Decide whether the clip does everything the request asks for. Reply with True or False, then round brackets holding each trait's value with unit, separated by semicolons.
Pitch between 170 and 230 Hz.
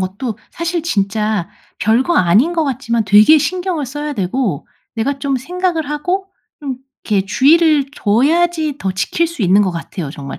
False (265 Hz)